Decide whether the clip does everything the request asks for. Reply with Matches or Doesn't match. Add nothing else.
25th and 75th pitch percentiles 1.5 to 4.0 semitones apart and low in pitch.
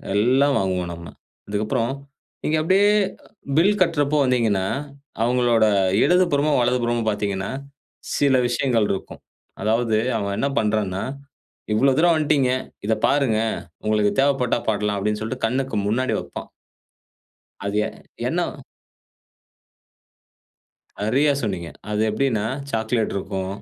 Doesn't match